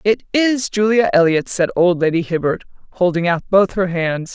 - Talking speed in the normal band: Yes, average, 180 wpm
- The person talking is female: Yes, female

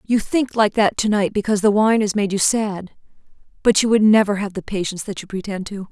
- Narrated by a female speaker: Yes, female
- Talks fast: Yes, fast, 245 wpm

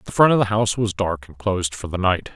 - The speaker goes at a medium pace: No, fast, 305 wpm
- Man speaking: Yes, male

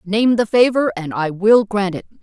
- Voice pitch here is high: Yes, high, 205 Hz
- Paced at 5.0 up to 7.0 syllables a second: No, 4.6 syllables/s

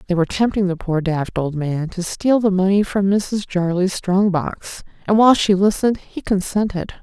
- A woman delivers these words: Yes, female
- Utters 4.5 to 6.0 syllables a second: Yes, 5.0 syllables/s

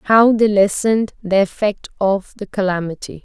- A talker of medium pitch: No, high, 200 Hz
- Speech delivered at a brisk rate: No, average, 150 wpm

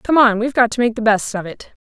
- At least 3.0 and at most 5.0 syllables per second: No, 6.4 syllables/s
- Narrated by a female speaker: Yes, female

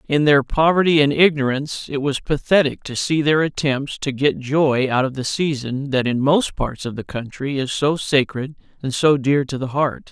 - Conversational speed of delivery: No, fast, 210 wpm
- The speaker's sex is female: No, male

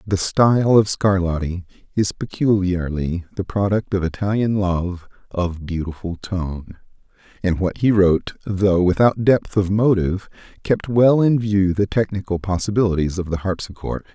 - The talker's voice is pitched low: Yes, very low, 95 Hz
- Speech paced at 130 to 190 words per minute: Yes, average, 140 wpm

